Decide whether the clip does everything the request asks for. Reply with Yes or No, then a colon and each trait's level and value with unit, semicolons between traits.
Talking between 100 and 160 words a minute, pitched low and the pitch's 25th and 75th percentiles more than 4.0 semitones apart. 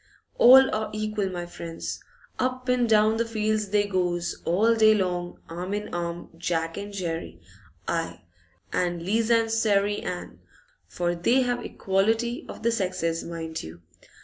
No: average, 150 wpm; high, 200 Hz; average, 4.4 semitones